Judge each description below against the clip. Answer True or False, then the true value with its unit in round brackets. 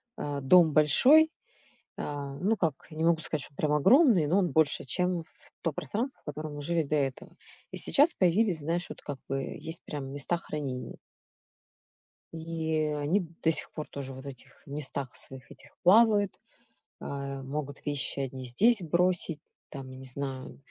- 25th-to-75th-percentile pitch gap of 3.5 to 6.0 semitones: True (4.1 semitones)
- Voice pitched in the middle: True (150 Hz)